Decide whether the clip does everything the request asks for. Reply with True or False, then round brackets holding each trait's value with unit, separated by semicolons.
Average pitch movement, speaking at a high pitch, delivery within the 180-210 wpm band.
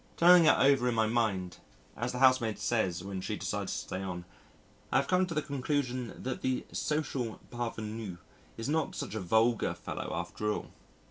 False (4.3 semitones; 120 Hz; 185 wpm)